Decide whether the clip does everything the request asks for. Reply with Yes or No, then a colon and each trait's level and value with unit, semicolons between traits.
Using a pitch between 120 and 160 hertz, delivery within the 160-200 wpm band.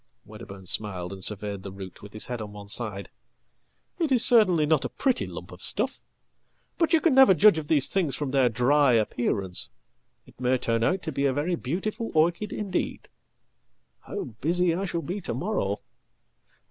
Yes: medium, 140 Hz; average, 170 wpm